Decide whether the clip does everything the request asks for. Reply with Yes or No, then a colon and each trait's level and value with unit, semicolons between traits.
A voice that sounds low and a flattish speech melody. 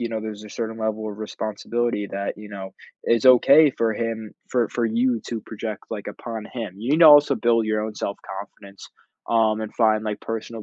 Yes: low, 110 Hz; narrow, 1.7 semitones